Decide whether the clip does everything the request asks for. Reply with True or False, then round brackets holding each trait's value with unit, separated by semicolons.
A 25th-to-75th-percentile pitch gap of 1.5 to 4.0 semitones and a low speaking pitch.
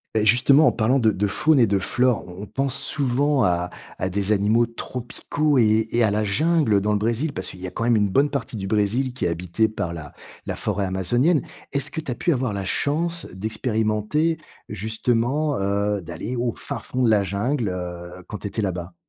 False (4.8 semitones; 110 Hz)